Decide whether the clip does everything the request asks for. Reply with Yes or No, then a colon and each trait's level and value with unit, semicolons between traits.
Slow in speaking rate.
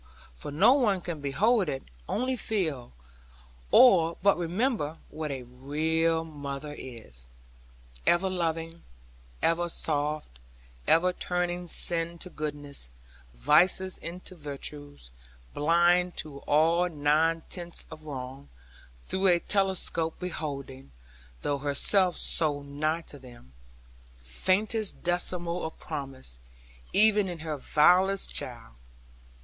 Yes: slow, 110 wpm